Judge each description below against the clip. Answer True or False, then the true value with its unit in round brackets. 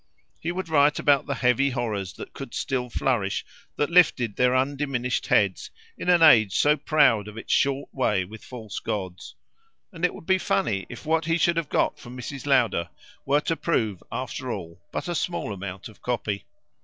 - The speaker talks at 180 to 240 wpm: True (190 wpm)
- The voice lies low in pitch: True (130 Hz)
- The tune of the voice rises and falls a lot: True (5.9 semitones)